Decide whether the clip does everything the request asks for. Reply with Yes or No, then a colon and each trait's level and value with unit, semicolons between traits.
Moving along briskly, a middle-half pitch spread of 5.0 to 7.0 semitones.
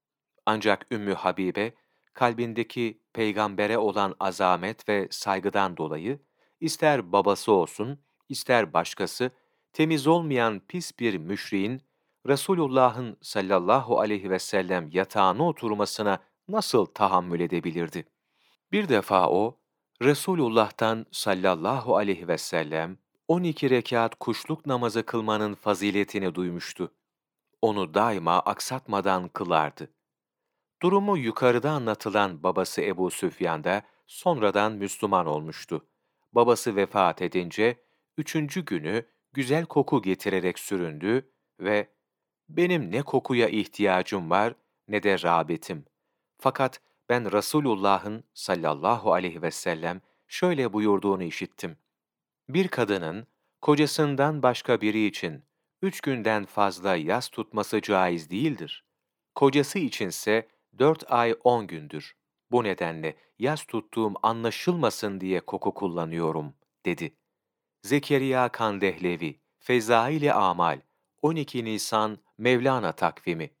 No: average, 100 wpm; wide, 5.4 semitones